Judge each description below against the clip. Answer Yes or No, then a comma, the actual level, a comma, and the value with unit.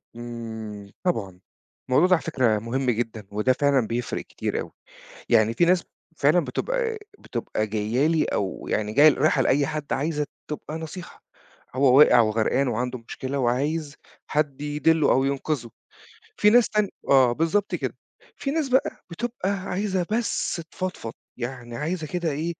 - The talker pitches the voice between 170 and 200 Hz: No, medium, 140 Hz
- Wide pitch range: Yes, wide, 6.0 semitones